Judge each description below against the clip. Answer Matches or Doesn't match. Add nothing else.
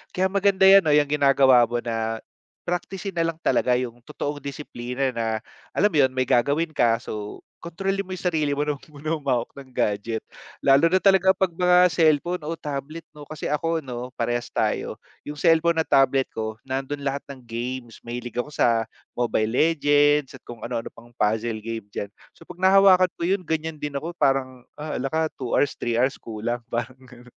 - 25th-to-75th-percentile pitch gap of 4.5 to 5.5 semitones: Matches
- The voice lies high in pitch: Doesn't match